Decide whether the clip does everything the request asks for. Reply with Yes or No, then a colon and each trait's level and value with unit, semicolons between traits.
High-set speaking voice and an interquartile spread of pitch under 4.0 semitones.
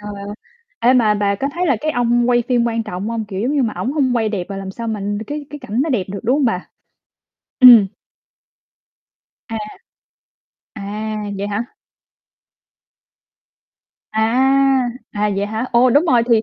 Yes: high, 235 Hz; average, 3.6 semitones